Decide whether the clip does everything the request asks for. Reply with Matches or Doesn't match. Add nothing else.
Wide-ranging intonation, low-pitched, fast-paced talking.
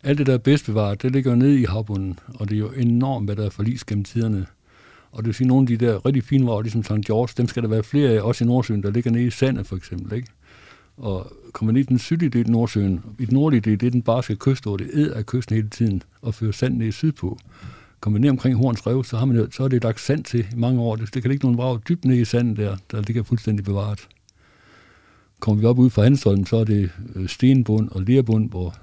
Doesn't match